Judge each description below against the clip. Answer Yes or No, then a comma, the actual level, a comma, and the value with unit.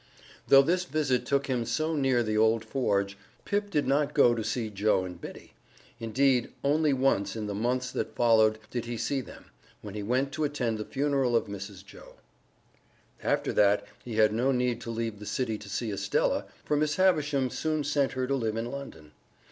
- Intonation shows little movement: No, average, 4.3 semitones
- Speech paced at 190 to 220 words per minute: Yes, average, 195 wpm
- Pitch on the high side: No, low, 125 Hz